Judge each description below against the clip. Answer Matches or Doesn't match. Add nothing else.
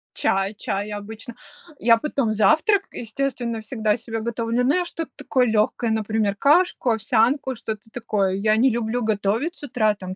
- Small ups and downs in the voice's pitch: Doesn't match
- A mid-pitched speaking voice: Doesn't match